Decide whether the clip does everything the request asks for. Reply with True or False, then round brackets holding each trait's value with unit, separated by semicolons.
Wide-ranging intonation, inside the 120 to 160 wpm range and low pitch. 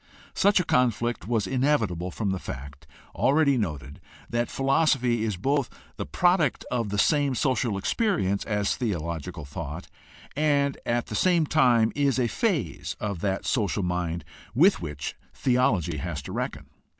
True (7.6 semitones; 150 wpm; 115 Hz)